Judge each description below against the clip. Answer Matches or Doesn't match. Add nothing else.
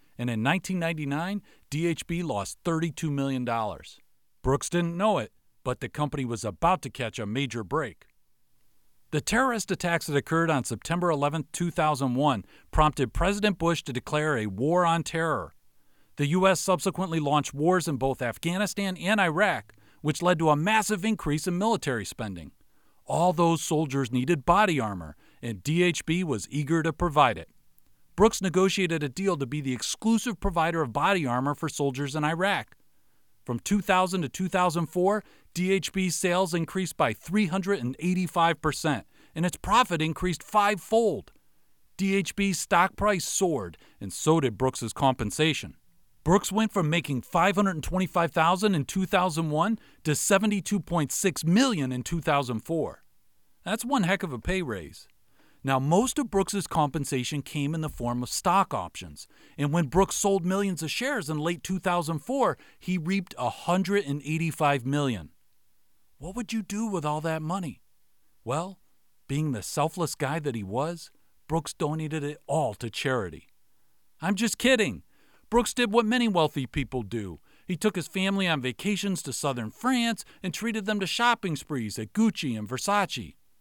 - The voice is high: Doesn't match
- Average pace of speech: Matches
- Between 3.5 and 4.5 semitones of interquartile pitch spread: Doesn't match